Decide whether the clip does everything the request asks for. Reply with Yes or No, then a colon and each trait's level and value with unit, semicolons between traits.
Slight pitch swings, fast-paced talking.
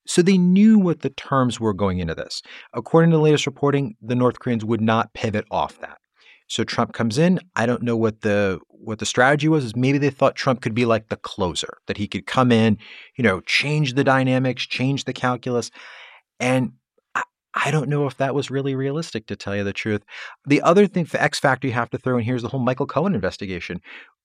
No: average, 4.1 semitones; fast, 230 wpm